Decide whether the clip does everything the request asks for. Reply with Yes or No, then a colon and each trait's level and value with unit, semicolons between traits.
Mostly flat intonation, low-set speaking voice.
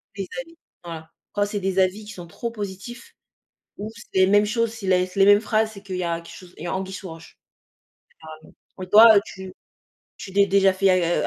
No: narrow, 2.2 semitones; high, 195 Hz